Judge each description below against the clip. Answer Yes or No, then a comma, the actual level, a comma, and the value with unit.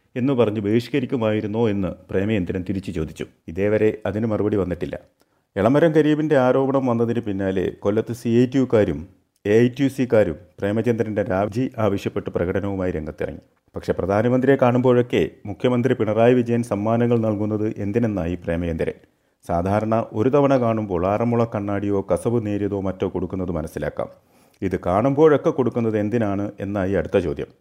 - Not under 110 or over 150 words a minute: Yes, fast, 125 wpm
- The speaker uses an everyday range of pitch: Yes, average, 3.6 semitones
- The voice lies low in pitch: Yes, low, 110 Hz